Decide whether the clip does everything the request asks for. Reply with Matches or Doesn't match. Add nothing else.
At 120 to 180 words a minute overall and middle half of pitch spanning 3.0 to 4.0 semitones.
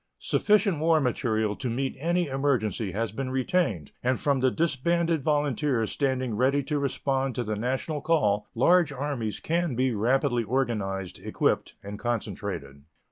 Doesn't match